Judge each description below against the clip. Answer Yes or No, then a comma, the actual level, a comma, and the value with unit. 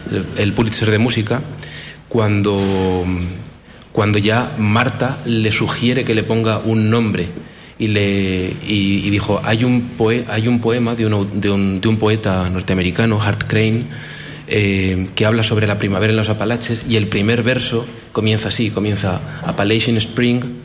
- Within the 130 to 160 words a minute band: Yes, average, 155 wpm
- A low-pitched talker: Yes, low, 110 Hz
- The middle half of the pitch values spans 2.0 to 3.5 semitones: Yes, narrow, 2.4 semitones